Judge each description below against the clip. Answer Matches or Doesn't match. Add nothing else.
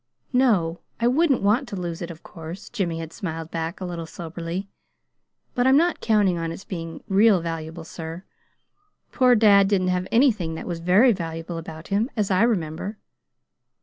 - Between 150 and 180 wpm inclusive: Matches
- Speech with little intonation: Doesn't match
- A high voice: Doesn't match